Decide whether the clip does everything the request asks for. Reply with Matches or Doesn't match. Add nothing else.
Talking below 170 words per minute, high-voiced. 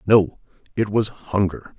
Doesn't match